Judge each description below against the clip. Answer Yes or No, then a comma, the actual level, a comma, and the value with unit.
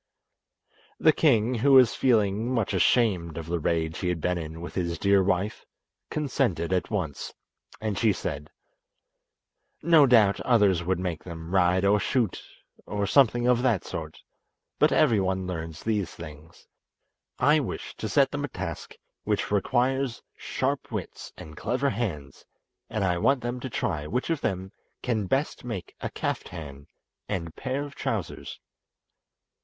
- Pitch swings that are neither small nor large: No, wide, 6.1 semitones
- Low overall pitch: Yes, low, 100 Hz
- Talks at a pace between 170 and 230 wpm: No, average, 155 wpm